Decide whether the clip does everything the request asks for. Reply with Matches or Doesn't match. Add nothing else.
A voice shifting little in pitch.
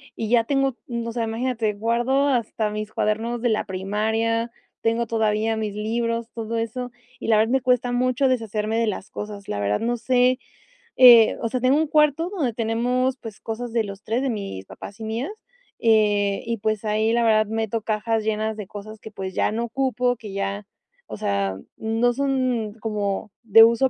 Matches